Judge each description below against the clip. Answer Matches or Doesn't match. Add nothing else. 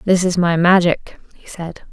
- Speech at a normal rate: Matches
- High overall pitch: Doesn't match